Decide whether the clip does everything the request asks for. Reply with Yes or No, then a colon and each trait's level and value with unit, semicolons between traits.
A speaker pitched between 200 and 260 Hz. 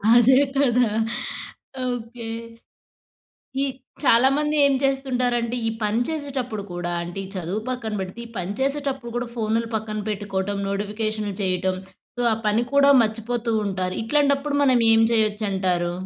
Yes: high, 225 Hz